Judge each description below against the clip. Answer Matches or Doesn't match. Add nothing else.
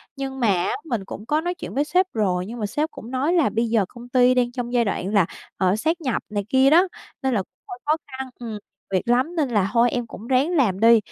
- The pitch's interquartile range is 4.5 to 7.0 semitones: Doesn't match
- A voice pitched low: Doesn't match